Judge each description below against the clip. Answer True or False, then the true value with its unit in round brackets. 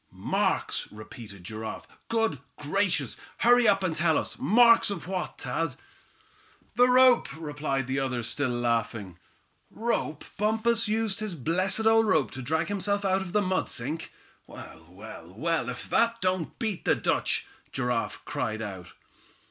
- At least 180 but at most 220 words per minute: False (150 wpm)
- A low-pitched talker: False (165 Hz)